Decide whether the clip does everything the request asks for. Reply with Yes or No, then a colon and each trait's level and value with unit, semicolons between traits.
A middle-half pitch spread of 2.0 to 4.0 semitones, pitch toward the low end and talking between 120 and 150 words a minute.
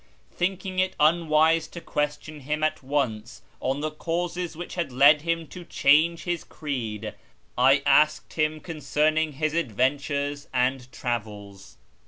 No: average, 3.7 semitones; medium, 150 Hz; average, 140 wpm